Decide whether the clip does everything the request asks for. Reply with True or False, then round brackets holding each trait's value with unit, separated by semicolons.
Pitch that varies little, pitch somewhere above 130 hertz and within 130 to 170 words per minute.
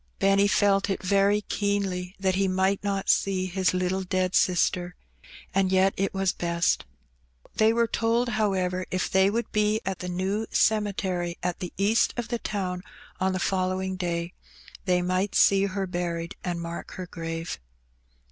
True (1.7 semitones; 190 Hz; 165 wpm)